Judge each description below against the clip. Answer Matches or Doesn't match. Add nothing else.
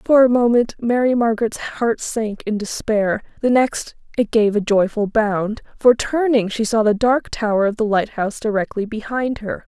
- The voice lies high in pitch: Matches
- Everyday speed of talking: Matches